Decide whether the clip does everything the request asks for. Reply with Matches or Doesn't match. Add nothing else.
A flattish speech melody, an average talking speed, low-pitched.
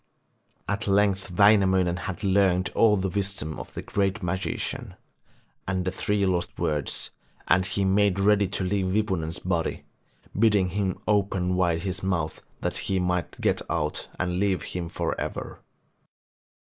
Matches